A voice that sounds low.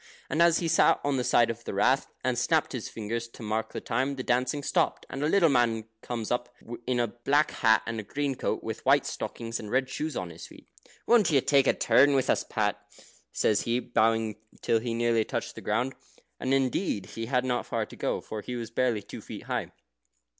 Yes: low, 120 Hz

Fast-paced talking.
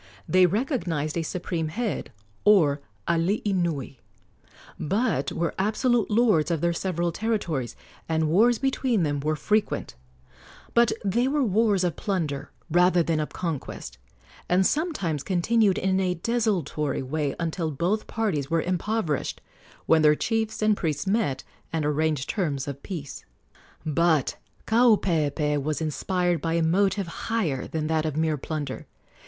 No: average, 140 wpm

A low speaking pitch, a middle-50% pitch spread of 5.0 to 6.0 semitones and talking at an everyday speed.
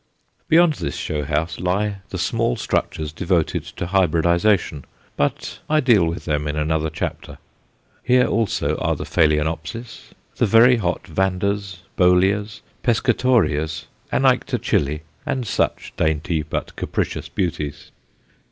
No: very low, 90 Hz; average, 5.3 semitones; slow, 120 wpm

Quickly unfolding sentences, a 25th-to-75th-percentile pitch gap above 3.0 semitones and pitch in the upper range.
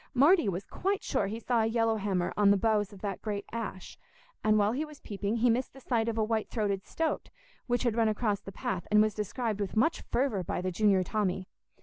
No: fast, 235 wpm; narrow, 2.6 semitones; high, 215 Hz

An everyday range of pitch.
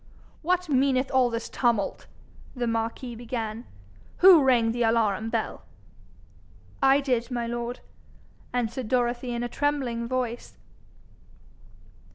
No: narrow, 2.1 semitones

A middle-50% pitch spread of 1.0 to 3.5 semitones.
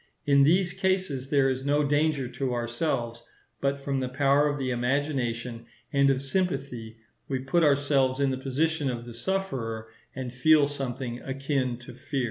Yes: narrow, 2.5 semitones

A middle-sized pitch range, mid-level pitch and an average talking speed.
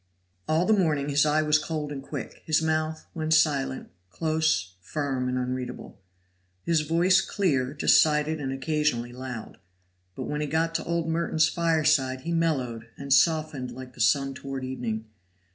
Yes: average, 3.5 semitones; medium, 150 Hz; average, 160 wpm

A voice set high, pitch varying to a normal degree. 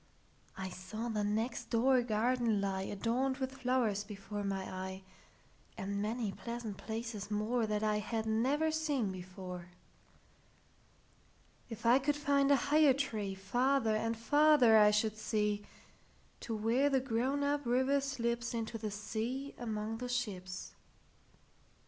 Yes: high, 225 Hz; average, 3.8 semitones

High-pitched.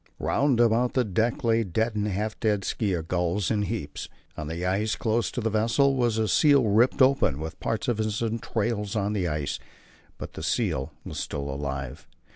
No: low, 105 Hz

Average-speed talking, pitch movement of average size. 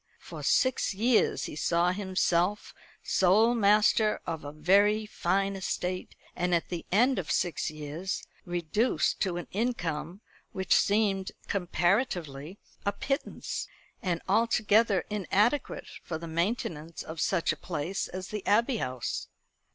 No: slow, 130 wpm; average, 3.7 semitones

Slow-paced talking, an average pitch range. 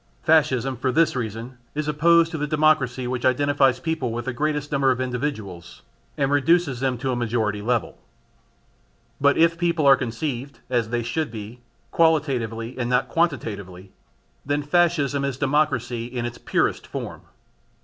No: average, 155 wpm; average, 3.8 semitones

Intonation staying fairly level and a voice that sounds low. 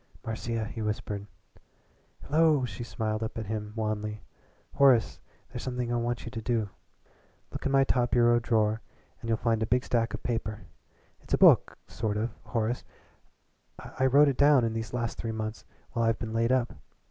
Yes: narrow, 1.9 semitones; low, 115 Hz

